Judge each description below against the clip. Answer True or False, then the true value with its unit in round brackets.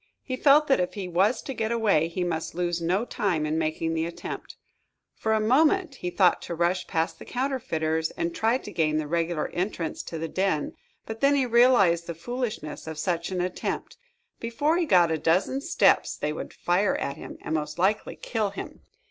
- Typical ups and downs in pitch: False (6.2 semitones)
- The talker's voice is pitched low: False (180 Hz)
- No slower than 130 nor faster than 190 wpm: False (200 wpm)